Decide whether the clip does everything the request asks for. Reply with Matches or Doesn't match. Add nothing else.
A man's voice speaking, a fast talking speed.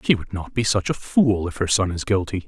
Matches